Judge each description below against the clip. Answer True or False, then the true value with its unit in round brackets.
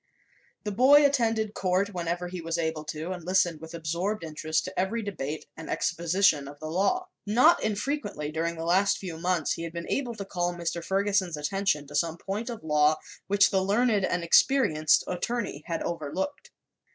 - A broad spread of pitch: False (4.0 semitones)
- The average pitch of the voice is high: False (180 Hz)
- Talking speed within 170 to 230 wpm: True (180 wpm)